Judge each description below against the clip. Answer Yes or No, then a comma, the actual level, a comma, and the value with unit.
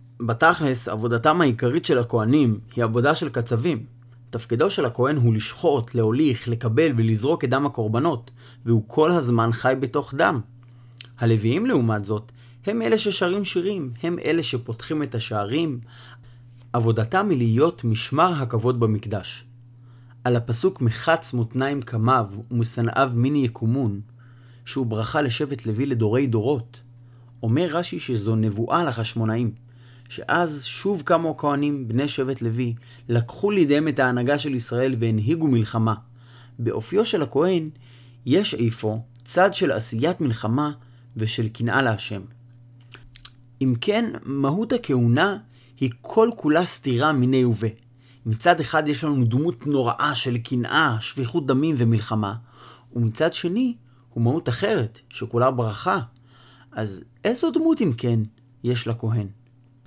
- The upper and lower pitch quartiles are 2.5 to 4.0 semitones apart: Yes, average, 3.6 semitones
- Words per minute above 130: No, average, 125 wpm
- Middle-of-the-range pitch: No, low, 120 Hz